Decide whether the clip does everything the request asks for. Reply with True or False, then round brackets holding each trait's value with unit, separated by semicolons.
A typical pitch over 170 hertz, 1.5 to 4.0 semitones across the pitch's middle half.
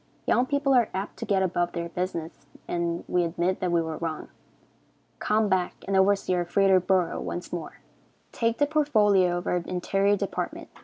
True (185 Hz; 2.8 semitones)